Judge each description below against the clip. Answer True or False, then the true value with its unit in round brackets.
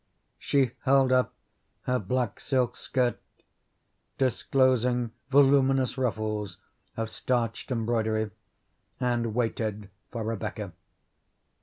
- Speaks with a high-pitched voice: False (120 Hz)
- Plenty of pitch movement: False (2.7 semitones)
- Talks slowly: True (90 wpm)